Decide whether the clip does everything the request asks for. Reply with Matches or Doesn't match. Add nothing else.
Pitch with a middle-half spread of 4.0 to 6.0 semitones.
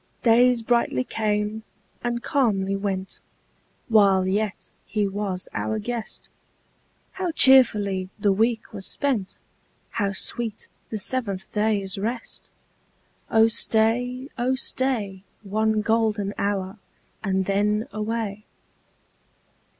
Doesn't match